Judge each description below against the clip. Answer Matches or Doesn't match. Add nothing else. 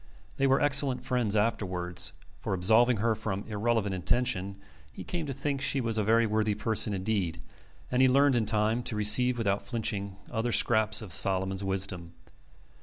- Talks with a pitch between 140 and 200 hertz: Doesn't match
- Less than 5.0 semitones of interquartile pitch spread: Matches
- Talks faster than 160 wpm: Matches